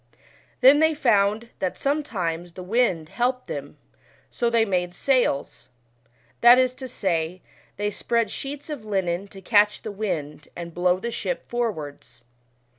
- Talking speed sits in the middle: Yes, average, 145 wpm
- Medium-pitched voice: No, high, 210 Hz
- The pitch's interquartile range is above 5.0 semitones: Yes, wide, 5.6 semitones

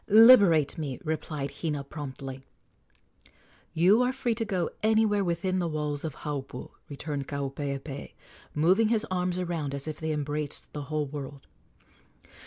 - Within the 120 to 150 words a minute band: Yes, average, 140 wpm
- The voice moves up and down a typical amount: Yes, average, 4.6 semitones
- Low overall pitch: No, medium, 155 Hz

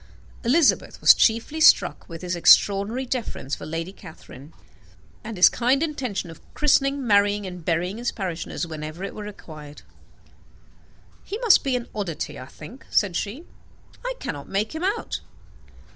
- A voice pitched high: Yes, high, 205 Hz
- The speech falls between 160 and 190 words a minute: No, average, 150 wpm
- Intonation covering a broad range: Yes, wide, 7.5 semitones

